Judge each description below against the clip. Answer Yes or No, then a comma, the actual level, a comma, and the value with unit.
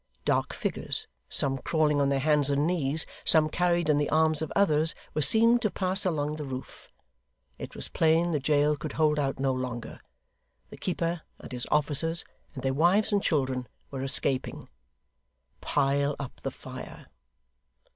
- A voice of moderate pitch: Yes, medium, 150 Hz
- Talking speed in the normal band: Yes, average, 165 wpm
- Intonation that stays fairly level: No, average, 3.0 semitones